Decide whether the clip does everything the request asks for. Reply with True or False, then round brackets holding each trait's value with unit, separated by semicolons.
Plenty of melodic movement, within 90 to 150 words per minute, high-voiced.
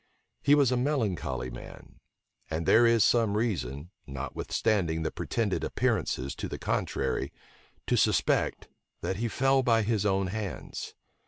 False (6.8 semitones; 140 wpm; 100 Hz)